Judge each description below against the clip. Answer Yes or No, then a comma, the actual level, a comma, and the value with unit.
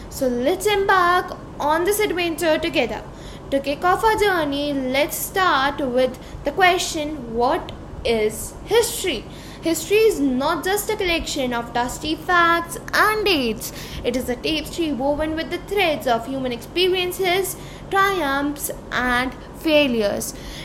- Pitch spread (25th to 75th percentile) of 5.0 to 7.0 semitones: Yes, average, 5.3 semitones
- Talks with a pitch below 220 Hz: No, very high, 315 Hz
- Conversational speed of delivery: No, slow, 130 wpm